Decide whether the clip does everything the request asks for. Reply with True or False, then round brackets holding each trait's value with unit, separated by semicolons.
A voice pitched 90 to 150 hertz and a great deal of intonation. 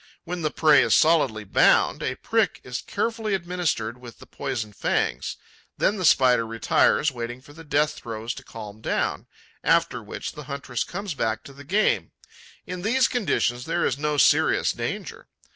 True (140 Hz; 6.6 semitones)